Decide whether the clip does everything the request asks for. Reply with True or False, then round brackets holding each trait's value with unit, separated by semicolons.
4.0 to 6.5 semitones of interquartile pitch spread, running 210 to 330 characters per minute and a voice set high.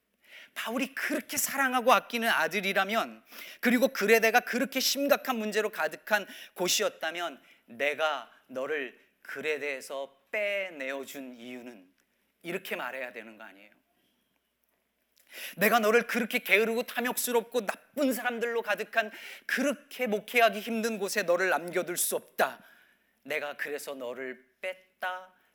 False (7.2 semitones; 290 characters per minute; 210 Hz)